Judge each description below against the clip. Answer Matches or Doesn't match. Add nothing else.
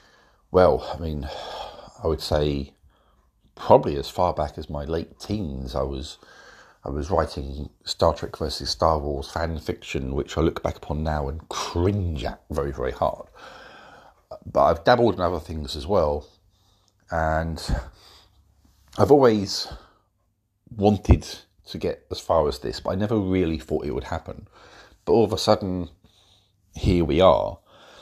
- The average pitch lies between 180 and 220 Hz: Doesn't match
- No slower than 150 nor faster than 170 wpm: Matches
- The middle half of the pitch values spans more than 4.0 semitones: Matches